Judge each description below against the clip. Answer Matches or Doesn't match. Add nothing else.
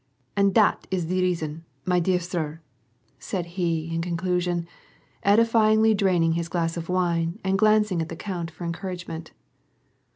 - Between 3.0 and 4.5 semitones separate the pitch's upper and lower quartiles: Doesn't match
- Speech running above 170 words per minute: Doesn't match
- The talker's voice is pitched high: Doesn't match